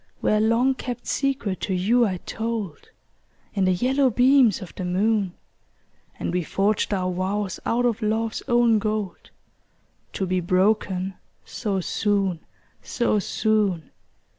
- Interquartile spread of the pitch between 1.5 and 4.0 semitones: Yes, average, 3.6 semitones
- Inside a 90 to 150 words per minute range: Yes, average, 140 wpm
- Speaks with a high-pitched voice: Yes, high, 210 Hz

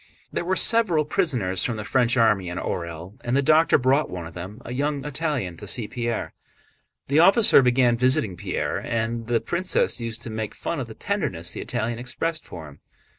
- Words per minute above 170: Yes, average, 195 wpm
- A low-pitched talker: Yes, low, 120 Hz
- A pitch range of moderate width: No, wide, 6.0 semitones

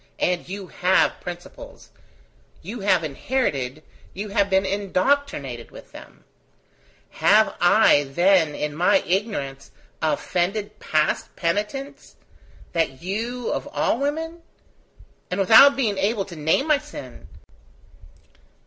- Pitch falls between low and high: No, high, 195 Hz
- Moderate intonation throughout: No, wide, 5.9 semitones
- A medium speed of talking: No, slow, 115 wpm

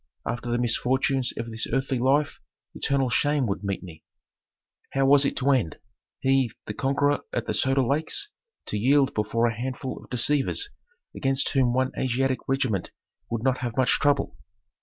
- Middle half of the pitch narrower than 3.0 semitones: Yes, narrow, 2.5 semitones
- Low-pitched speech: Yes, low, 130 Hz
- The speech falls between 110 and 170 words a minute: Yes, average, 165 wpm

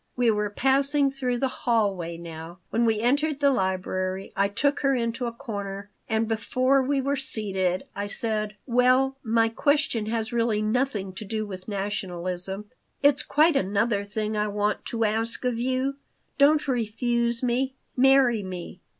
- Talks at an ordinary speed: Yes, average, 160 wpm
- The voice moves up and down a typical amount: Yes, average, 4.4 semitones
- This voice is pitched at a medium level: No, high, 225 Hz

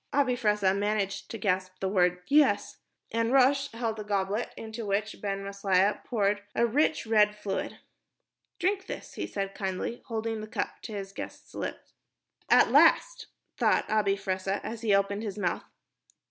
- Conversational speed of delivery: Yes, average, 160 wpm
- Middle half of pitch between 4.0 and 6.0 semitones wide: No, narrow, 2.5 semitones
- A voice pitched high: Yes, high, 210 Hz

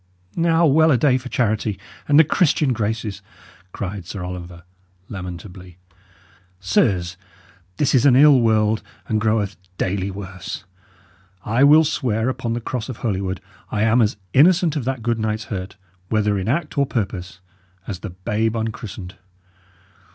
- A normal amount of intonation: Yes, average, 5.0 semitones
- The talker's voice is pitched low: Yes, low, 110 Hz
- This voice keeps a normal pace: Yes, average, 150 wpm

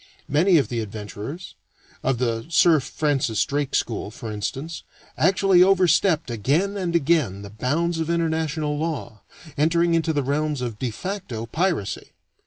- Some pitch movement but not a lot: No, wide, 6.2 semitones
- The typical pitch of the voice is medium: Yes, medium, 150 Hz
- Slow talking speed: No, average, 145 wpm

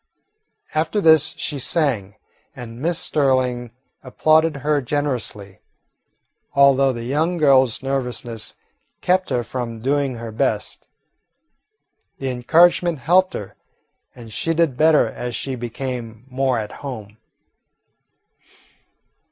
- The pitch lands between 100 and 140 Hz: Yes, low, 135 Hz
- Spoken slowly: Yes, slow, 110 wpm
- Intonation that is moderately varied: Yes, average, 4.1 semitones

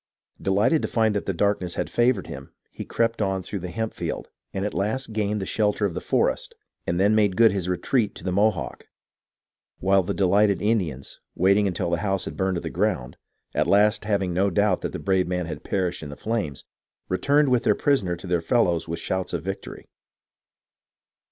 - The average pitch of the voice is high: No, very low, 95 Hz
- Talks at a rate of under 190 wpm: No, average, 200 wpm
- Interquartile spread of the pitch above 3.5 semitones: No, average, 2.9 semitones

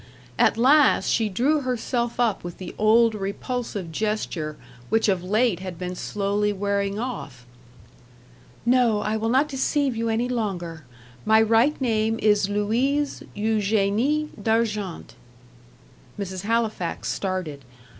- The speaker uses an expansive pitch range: No, average, 3.2 semitones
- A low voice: No, high, 215 Hz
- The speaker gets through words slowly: Yes, slow, 125 wpm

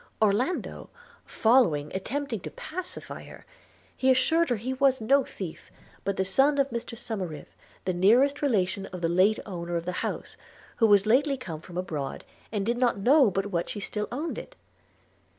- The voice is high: Yes, high, 220 Hz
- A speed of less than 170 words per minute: No, average, 175 wpm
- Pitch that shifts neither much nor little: No, wide, 6.1 semitones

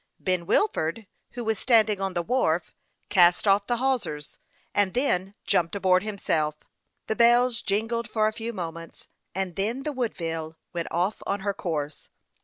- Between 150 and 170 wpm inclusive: Yes, average, 160 wpm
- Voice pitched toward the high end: Yes, high, 200 Hz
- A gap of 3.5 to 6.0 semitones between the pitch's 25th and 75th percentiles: Yes, average, 4.8 semitones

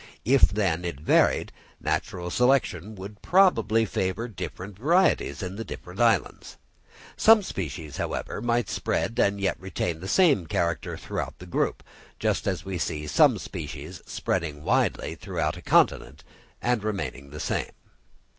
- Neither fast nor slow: Yes, average, 145 wpm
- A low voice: Yes, very low, 95 Hz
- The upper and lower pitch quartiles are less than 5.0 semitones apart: No, average, 5.3 semitones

